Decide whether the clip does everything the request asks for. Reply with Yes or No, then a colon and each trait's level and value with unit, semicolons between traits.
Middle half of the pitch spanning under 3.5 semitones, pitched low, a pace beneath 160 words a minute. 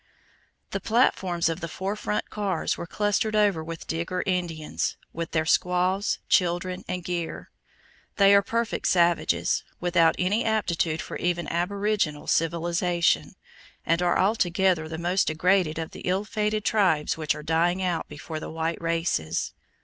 No: average, 3.0 semitones; medium, 175 Hz; average, 150 wpm